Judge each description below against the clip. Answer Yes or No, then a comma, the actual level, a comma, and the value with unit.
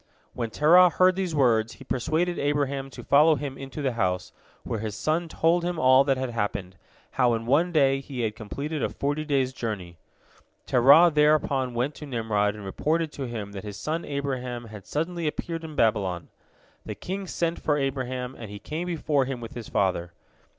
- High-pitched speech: No, low, 135 Hz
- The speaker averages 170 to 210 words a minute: Yes, average, 185 wpm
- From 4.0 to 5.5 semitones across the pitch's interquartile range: Yes, average, 5.2 semitones